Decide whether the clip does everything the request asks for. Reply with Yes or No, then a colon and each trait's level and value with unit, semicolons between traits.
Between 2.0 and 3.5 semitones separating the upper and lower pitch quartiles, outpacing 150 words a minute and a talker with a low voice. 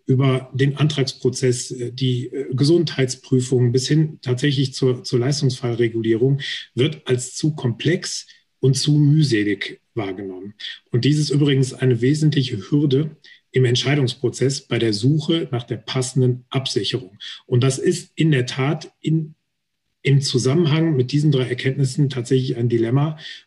No: average, 2.7 semitones; average, 130 wpm; low, 130 Hz